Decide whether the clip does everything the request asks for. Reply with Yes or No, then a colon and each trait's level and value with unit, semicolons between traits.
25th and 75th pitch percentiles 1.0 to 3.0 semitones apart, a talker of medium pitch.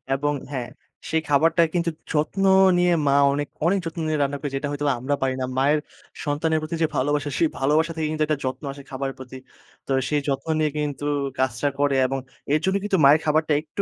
Yes: narrow, 2.4 semitones; medium, 145 Hz